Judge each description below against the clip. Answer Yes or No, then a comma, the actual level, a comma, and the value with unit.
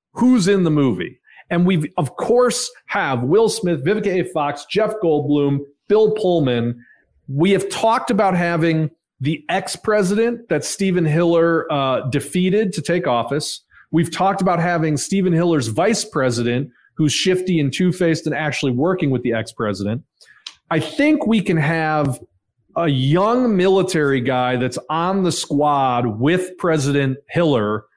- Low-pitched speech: No, medium, 165 Hz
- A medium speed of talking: Yes, average, 145 wpm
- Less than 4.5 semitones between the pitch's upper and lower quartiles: No, average, 5.0 semitones